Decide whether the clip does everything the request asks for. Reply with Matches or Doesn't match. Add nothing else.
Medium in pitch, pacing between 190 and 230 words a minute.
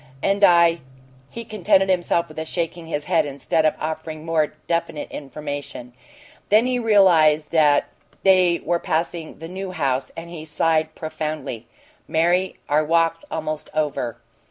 Doesn't match